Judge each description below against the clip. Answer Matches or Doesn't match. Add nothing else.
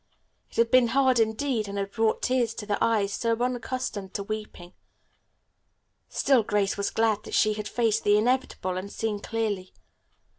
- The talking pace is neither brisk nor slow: Matches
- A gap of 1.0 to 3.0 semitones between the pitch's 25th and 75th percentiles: Matches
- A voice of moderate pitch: Doesn't match